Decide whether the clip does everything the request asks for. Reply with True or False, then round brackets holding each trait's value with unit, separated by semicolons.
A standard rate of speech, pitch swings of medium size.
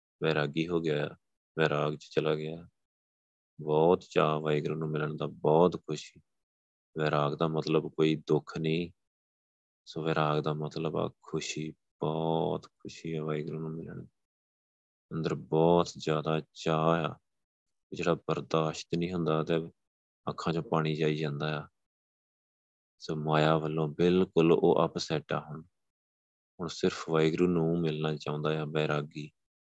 False (130 wpm; 1.2 semitones)